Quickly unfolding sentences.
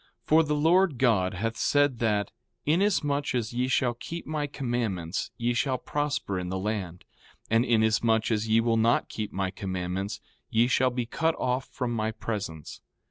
No: average, 175 wpm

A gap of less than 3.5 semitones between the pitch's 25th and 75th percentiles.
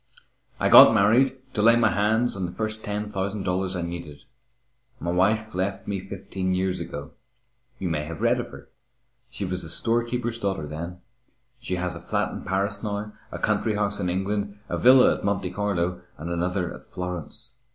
Yes: average, 2.8 semitones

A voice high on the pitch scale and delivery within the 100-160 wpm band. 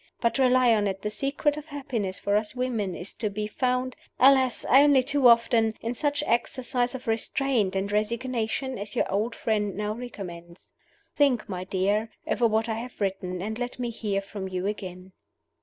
No: high, 225 Hz; average, 180 wpm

